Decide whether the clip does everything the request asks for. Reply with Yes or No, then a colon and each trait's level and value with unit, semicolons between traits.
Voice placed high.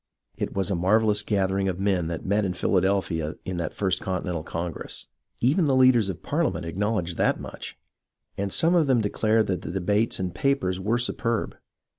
No: low, 100 Hz